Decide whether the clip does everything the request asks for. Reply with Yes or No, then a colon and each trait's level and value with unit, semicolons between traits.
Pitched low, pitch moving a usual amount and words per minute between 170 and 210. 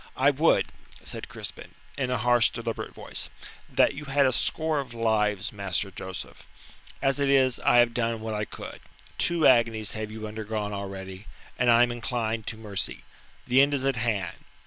Yes: low, 115 Hz; average, 3.4 semitones; average, 180 wpm